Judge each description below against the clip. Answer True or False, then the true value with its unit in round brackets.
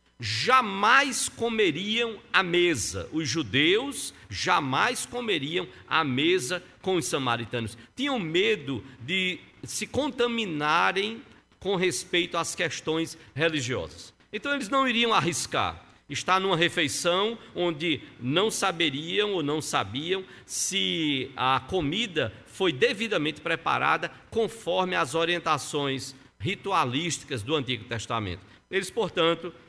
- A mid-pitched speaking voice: True (175 Hz)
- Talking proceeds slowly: True (105 wpm)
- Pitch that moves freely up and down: True (6.3 semitones)